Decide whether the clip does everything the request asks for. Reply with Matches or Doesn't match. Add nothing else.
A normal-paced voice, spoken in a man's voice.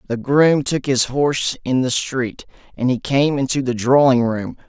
Matches